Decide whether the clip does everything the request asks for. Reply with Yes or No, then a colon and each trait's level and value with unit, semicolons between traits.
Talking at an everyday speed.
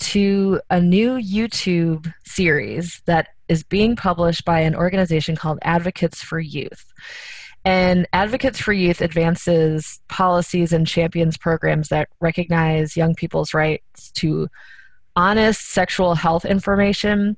No: slow, 120 wpm